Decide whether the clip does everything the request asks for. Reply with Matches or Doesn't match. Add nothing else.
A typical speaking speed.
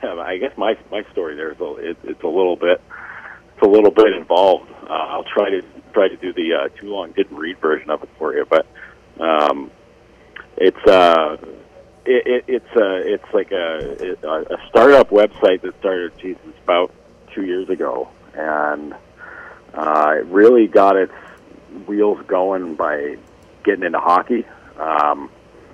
Matches